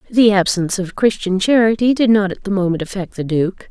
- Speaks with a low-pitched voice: No, high, 195 Hz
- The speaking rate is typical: No, fast, 210 wpm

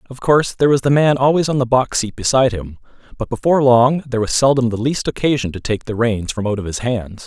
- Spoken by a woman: No, male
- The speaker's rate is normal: No, fast, 255 wpm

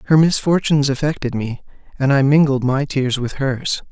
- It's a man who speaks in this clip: Yes, male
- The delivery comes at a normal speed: Yes, average, 170 wpm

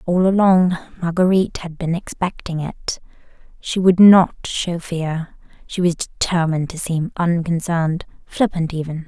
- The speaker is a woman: Yes, female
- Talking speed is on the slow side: Yes, slow, 130 wpm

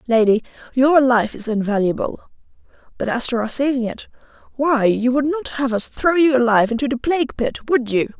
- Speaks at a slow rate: No, average, 190 wpm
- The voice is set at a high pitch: Yes, very high, 250 Hz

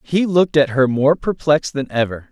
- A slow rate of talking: No, fast, 205 wpm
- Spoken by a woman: No, male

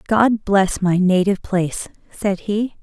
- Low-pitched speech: No, high, 195 Hz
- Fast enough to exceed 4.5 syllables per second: No, 4.3 syllables/s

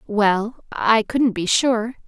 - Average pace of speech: Yes, average, 145 wpm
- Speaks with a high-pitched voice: Yes, high, 220 Hz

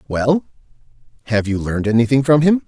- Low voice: Yes, low, 125 Hz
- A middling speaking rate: Yes, average, 155 wpm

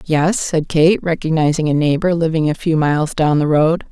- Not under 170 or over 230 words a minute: Yes, average, 200 wpm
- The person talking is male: No, female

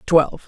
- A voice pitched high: No, medium, 160 Hz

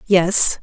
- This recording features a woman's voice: Yes, female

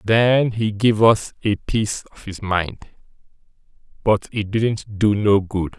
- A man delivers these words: Yes, male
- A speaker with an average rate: Yes, average, 155 wpm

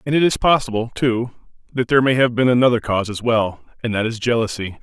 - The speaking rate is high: Yes, fast, 225 wpm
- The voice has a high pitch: No, low, 120 Hz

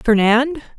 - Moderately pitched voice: No, very high, 250 Hz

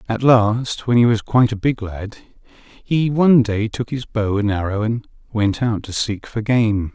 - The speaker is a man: Yes, male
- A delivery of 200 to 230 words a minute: Yes, fast, 205 wpm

